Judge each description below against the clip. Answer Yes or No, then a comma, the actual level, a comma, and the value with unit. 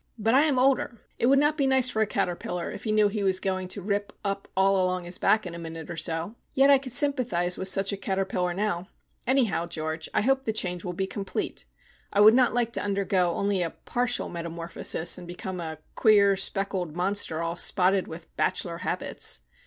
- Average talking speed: No, fast, 210 wpm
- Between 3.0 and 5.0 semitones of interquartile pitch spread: Yes, average, 3.8 semitones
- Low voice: No, high, 195 Hz